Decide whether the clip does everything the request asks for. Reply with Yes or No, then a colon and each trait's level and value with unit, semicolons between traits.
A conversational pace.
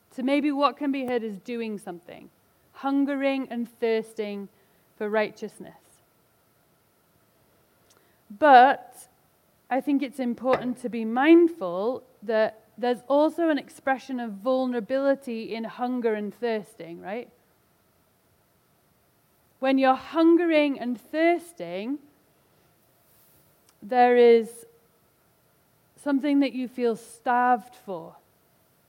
No: slow, 100 wpm